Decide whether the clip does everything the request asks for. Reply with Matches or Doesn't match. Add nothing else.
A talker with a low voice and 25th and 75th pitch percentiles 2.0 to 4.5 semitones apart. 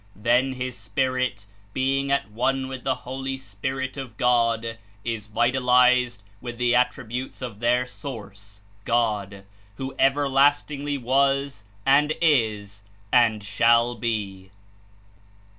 Matches